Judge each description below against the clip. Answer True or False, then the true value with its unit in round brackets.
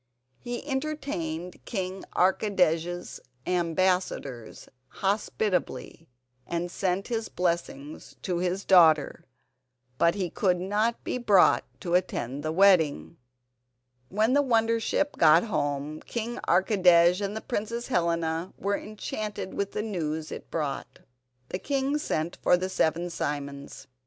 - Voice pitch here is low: False (180 Hz)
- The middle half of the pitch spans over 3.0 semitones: True (4.4 semitones)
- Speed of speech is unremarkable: False (120 wpm)